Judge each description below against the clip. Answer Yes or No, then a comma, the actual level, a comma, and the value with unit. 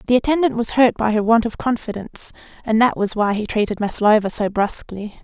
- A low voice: No, high, 220 Hz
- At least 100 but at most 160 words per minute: No, fast, 205 wpm